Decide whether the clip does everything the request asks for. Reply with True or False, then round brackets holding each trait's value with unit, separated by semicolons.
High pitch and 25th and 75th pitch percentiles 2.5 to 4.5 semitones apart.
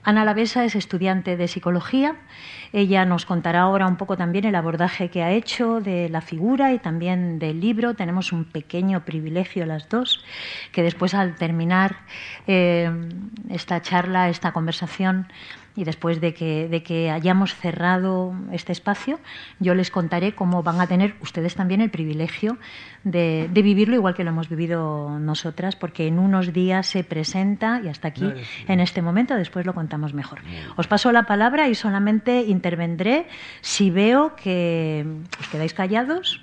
False (180 Hz; 3.2 semitones)